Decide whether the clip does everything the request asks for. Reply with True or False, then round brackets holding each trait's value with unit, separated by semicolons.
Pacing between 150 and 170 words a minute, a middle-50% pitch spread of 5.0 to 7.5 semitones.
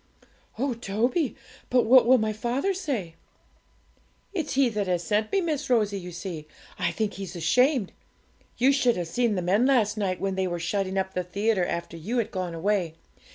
False (190 wpm; 5.3 semitones)